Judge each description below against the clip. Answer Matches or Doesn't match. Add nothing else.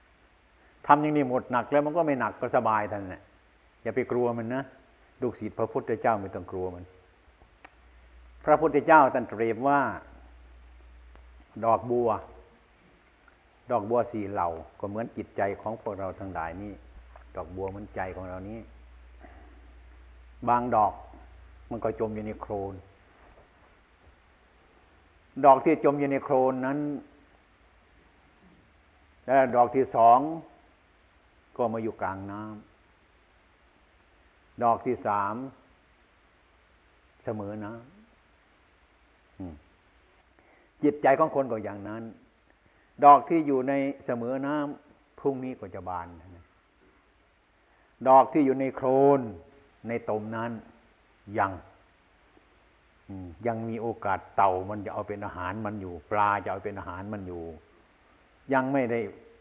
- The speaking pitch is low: Matches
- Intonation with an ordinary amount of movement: Doesn't match